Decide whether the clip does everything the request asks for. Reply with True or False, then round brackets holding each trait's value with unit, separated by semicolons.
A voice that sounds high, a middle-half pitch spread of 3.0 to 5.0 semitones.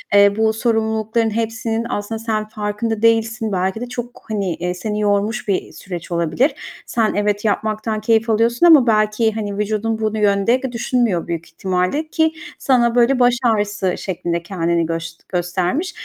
False (215 Hz; 2.6 semitones)